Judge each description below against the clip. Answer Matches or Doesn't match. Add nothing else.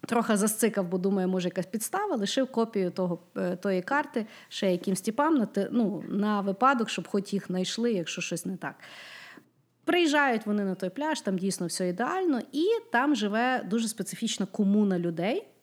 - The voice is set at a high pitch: Matches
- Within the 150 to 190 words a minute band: Matches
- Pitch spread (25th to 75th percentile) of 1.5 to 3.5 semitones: Doesn't match